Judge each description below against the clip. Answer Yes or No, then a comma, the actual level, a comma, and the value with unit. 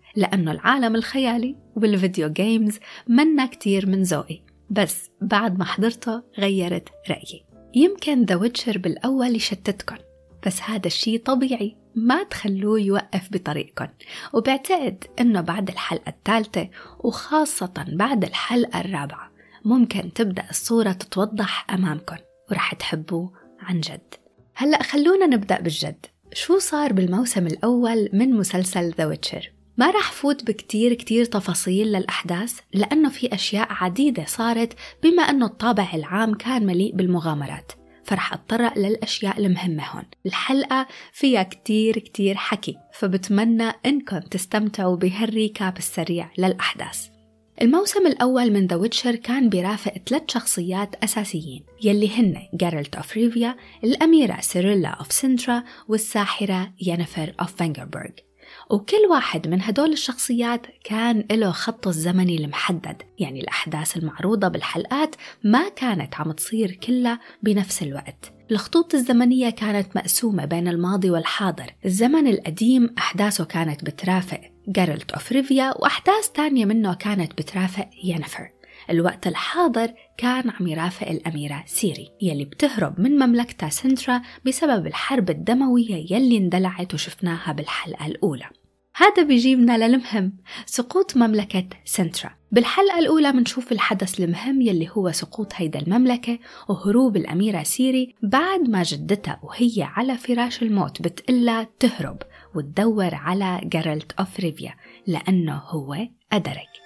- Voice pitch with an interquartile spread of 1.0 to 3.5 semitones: No, average, 5.2 semitones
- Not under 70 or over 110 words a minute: No, average, 120 wpm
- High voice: Yes, high, 210 Hz